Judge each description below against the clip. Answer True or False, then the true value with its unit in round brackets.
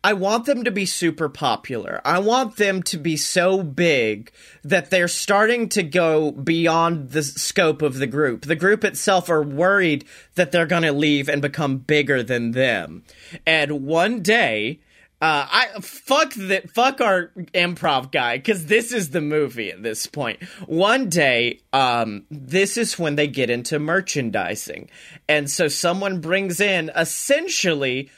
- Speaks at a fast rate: False (160 wpm)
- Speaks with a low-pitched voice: False (170 Hz)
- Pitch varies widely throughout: False (4.8 semitones)